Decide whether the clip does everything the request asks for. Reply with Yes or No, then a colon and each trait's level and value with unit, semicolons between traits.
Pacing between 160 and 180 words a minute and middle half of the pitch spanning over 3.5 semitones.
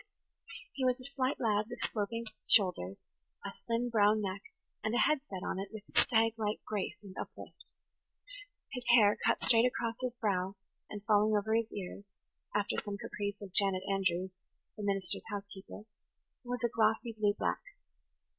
No: average, 165 wpm; narrow, 2.5 semitones